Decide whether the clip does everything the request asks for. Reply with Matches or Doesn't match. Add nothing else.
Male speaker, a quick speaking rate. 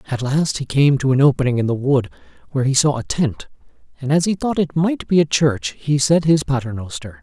Matches